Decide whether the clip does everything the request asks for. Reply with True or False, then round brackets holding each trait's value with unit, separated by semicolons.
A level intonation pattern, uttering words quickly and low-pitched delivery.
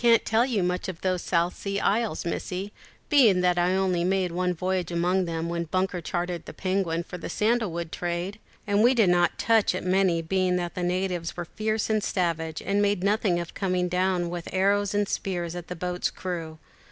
False (2.3 semitones; 215 wpm; 180 Hz)